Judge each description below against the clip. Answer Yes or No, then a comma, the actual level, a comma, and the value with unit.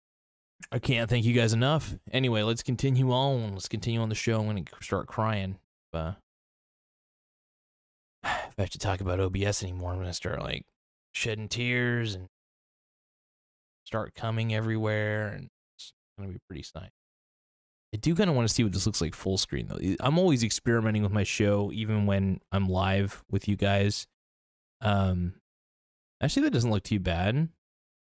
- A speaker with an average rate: Yes, average, 165 wpm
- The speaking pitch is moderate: No, low, 105 Hz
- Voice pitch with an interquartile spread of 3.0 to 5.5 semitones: Yes, average, 3.6 semitones